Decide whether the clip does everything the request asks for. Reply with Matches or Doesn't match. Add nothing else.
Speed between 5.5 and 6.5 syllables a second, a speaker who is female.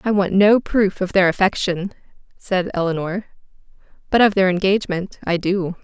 Doesn't match